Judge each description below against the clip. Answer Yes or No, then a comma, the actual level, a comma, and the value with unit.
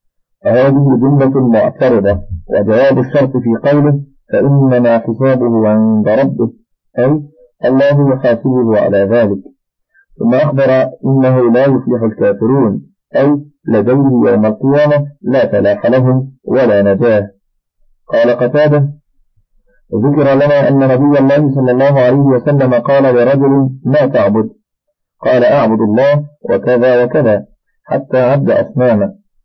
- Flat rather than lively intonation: No, average, 3.1 semitones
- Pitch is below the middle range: Yes, low, 130 Hz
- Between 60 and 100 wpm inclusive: No, average, 110 wpm